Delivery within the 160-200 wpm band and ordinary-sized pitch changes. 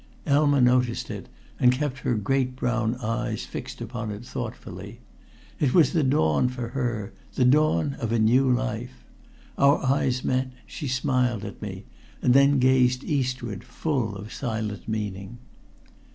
No: average, 150 wpm; average, 3.2 semitones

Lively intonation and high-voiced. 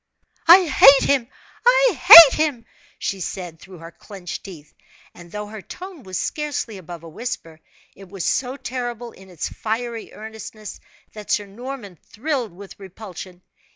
Yes: wide, 5.9 semitones; high, 215 Hz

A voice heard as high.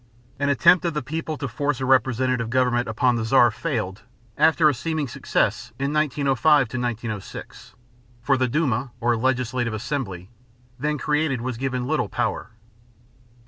No: low, 130 Hz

